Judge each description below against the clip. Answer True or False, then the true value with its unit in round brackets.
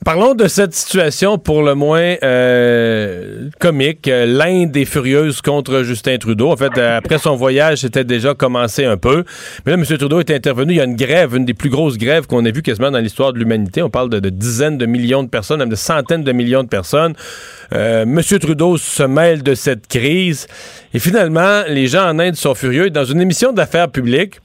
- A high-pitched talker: False (140 Hz)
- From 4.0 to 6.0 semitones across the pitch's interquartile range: True (4.6 semitones)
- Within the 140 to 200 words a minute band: False (210 wpm)